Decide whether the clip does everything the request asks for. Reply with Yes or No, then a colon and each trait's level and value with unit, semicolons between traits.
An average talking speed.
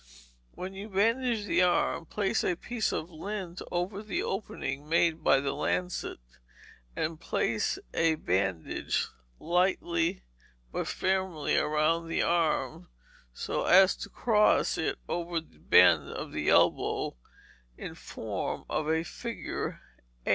No: slow, 130 wpm